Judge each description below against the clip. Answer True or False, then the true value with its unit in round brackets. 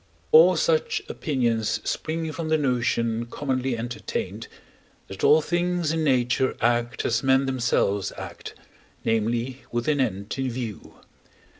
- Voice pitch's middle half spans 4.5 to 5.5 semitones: True (4.8 semitones)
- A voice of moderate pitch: False (130 Hz)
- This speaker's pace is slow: True (130 wpm)